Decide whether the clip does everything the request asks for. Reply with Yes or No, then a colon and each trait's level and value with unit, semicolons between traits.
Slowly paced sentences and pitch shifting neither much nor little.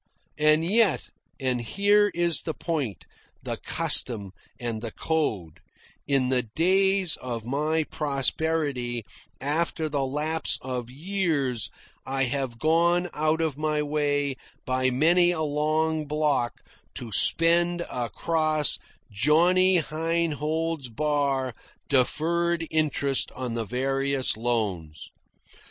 Yes: slow, 110 wpm; average, 4.2 semitones